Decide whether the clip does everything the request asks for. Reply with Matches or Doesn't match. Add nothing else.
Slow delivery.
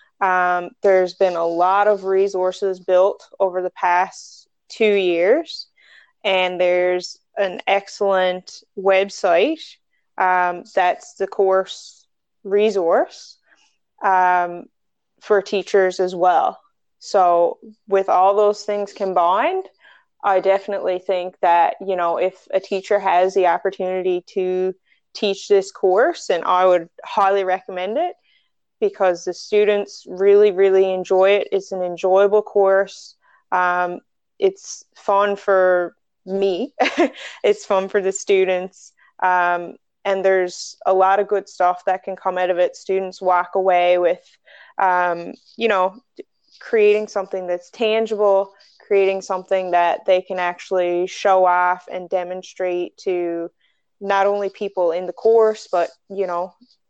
Matches